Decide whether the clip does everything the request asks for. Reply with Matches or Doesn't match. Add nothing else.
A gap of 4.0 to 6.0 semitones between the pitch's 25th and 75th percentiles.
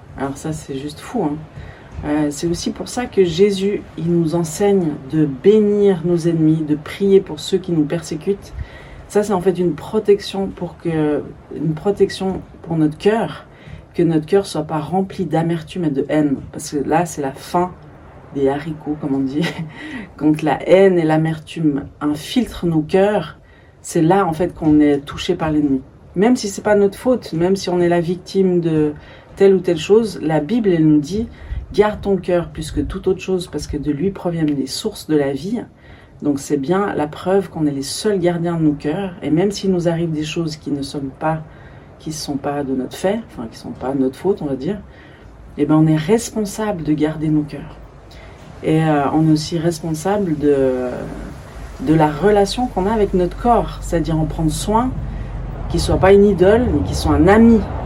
Matches